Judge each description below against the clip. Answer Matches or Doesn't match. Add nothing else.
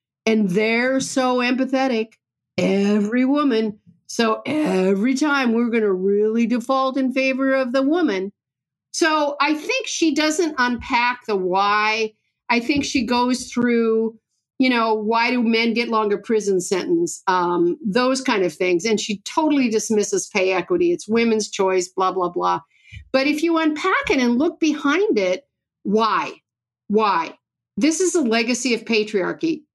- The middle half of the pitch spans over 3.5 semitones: Matches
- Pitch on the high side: Matches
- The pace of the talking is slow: Doesn't match